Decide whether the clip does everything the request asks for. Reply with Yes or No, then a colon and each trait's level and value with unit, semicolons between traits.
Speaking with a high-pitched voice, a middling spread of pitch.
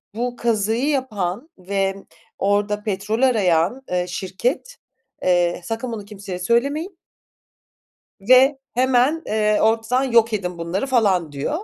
Yes: high, 220 Hz; average, 4.7 semitones